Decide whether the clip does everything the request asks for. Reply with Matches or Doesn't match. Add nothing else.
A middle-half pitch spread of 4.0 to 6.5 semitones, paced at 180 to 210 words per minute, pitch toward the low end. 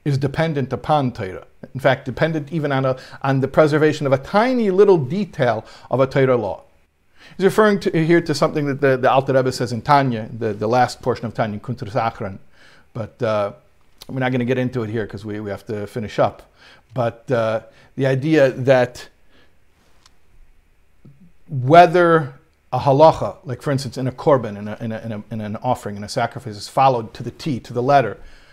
Matches